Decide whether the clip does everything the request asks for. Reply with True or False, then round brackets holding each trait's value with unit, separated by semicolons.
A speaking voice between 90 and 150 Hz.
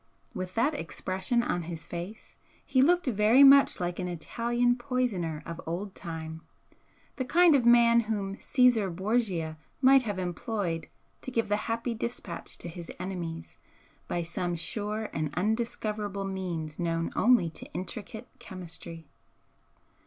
False (200 Hz)